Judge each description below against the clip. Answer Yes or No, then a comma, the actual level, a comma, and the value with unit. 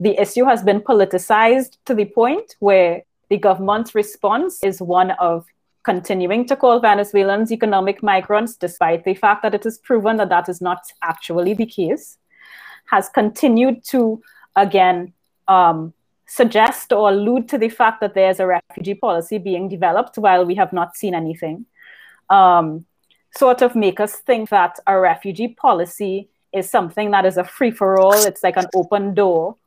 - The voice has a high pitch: Yes, high, 200 Hz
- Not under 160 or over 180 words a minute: Yes, average, 170 wpm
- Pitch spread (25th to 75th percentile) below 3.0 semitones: No, average, 3.5 semitones